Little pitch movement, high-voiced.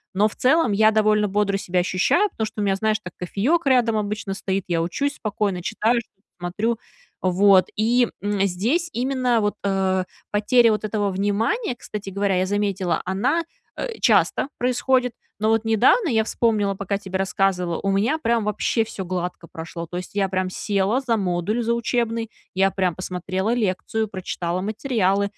No: average, 3.3 semitones; high, 205 Hz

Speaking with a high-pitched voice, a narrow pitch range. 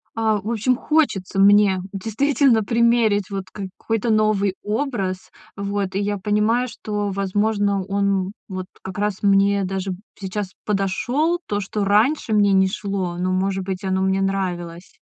Yes: high, 200 Hz; narrow, 2.1 semitones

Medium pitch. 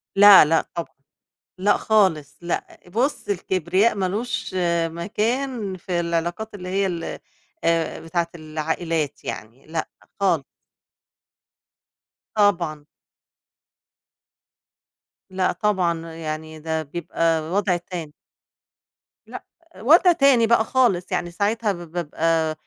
Yes: medium, 175 Hz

